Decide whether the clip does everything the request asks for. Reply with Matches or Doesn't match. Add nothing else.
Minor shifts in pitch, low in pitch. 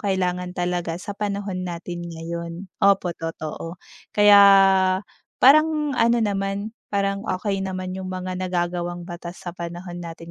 Doesn't match